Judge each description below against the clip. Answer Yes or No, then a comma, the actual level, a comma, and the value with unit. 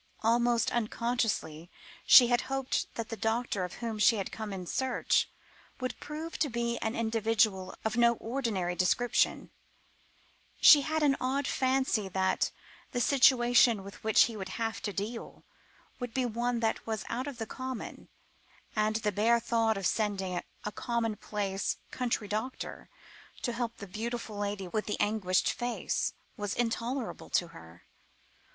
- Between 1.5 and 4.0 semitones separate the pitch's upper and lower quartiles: Yes, average, 2.8 semitones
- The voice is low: No, high, 225 Hz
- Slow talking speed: No, average, 150 wpm